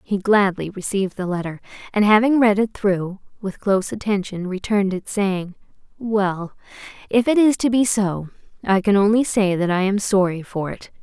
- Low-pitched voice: No, high, 200 Hz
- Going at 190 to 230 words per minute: No, average, 180 wpm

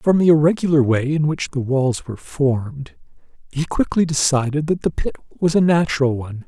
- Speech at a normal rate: Yes, average, 185 wpm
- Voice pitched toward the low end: No, medium, 145 Hz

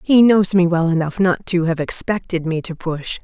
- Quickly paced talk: Yes, fast, 220 wpm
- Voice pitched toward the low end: No, medium, 175 Hz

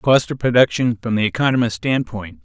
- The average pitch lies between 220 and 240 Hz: No, low, 115 Hz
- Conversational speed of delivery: Yes, average, 170 wpm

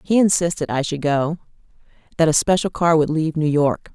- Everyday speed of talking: Yes, average, 180 wpm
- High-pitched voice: No, medium, 160 Hz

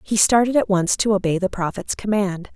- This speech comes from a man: No, female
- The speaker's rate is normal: No, fast, 210 wpm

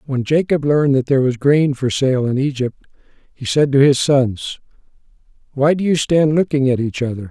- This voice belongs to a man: Yes, male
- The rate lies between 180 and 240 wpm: Yes, average, 195 wpm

